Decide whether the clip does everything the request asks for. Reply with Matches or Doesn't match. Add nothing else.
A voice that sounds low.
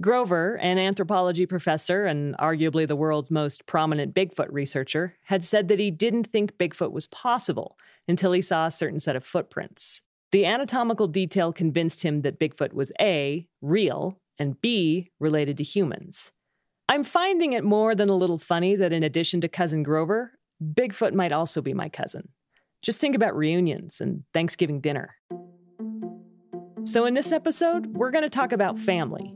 Doesn't match